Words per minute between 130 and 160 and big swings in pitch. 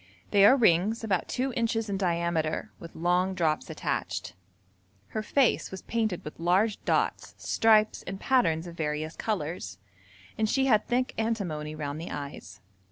Yes: average, 155 wpm; wide, 5.7 semitones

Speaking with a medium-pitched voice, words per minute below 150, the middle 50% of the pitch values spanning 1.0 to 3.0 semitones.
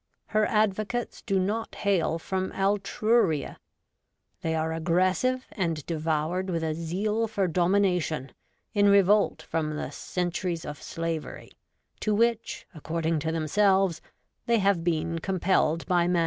No: medium, 180 Hz; average, 140 wpm; average, 3.7 semitones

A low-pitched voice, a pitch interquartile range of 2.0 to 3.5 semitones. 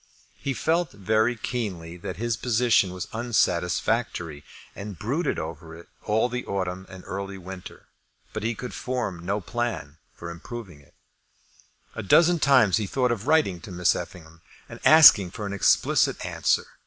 No: low, 100 Hz; average, 5.3 semitones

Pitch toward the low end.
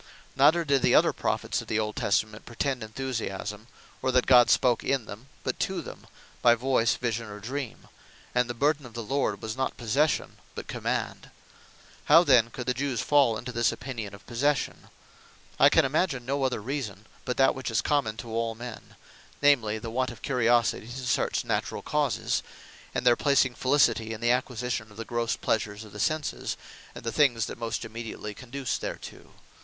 Yes: low, 120 Hz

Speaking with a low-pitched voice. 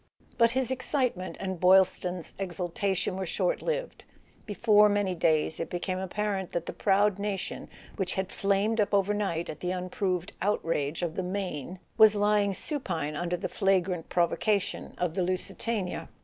No: high, 190 Hz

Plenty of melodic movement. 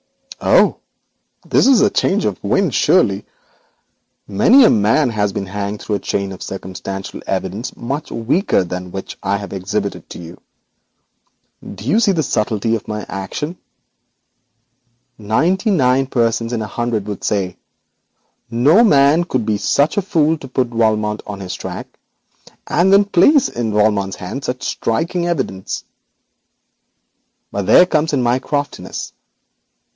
Yes: wide, 7.0 semitones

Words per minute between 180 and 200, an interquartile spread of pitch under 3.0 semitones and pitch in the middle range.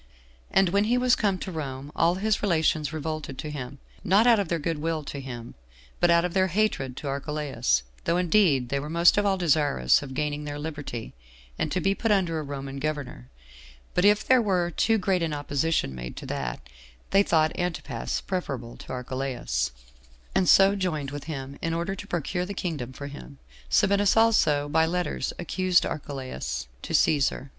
No: average, 185 wpm; average, 5.0 semitones; medium, 155 Hz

